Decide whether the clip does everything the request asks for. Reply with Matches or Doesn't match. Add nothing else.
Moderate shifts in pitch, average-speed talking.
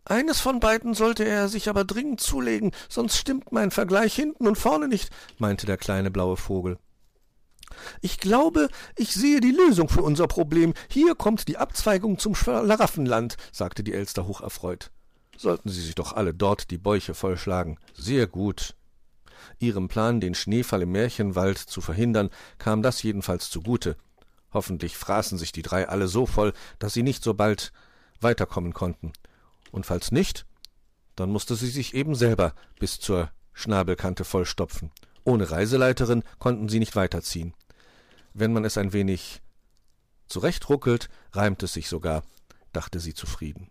Doesn't match